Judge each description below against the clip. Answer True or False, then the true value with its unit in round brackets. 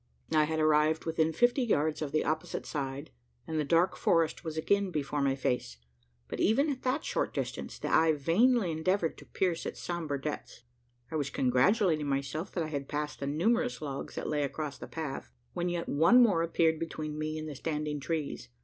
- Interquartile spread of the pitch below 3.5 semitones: True (2.7 semitones)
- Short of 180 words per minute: False (195 wpm)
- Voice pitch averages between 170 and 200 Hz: False (155 Hz)